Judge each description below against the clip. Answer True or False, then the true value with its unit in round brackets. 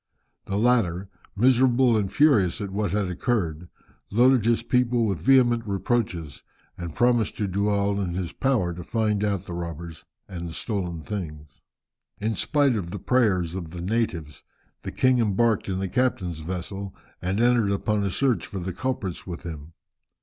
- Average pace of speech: True (170 wpm)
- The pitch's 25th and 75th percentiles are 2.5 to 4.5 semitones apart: False (5.1 semitones)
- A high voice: False (100 Hz)